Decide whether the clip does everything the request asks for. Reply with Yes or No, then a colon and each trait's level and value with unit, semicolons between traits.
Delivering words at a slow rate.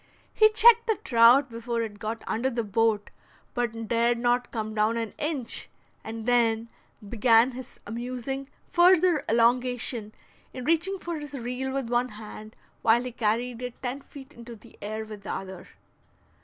No: average, 160 wpm